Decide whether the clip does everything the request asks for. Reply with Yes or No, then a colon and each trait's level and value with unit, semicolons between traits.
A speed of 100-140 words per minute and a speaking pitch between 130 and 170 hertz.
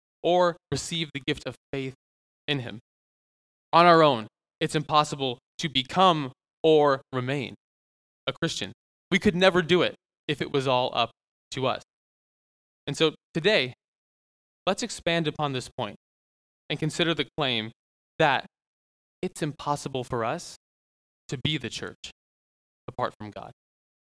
Yes: slow, 135 wpm; medium, 140 Hz